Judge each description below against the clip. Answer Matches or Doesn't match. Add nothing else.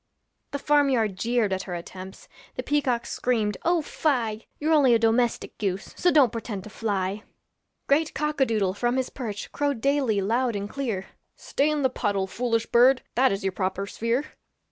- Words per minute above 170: Matches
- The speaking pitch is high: Matches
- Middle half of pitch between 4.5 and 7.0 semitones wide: Matches